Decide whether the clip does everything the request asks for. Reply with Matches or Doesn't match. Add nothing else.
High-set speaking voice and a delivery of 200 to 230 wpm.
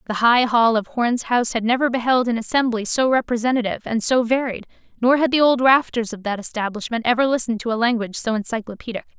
Matches